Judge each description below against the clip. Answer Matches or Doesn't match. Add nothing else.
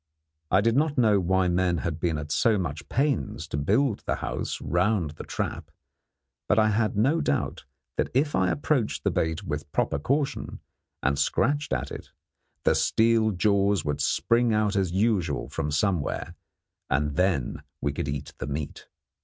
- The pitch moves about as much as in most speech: Doesn't match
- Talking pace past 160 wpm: Matches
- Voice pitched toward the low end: Matches